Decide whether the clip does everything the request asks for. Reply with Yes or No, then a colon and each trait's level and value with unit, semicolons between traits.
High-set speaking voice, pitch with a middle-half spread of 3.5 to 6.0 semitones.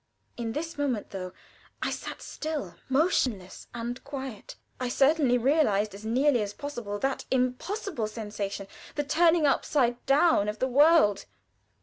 Yes: very high, 255 Hz; wide, 5.5 semitones